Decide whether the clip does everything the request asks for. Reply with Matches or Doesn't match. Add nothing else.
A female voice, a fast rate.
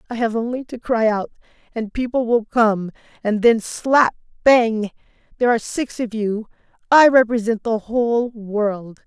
Doesn't match